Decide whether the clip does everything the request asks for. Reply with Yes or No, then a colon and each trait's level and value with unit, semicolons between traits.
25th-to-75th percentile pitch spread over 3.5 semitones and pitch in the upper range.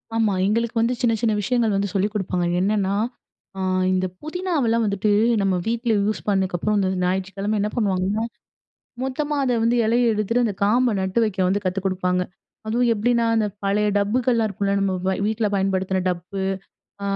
No: average, 3.2 semitones; high, 210 Hz